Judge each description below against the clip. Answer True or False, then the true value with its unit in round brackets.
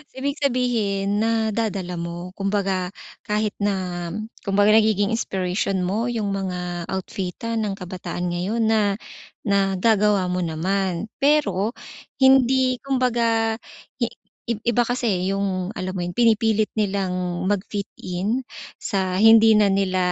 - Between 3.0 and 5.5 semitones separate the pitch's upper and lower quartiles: True (3.4 semitones)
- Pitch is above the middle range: True (200 Hz)